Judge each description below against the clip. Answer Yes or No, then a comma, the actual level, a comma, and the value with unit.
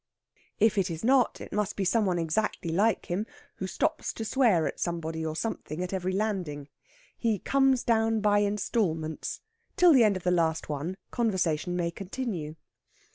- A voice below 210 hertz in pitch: Yes, high, 190 Hz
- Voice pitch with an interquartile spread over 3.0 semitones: Yes, average, 4.9 semitones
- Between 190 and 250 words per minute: No, average, 175 wpm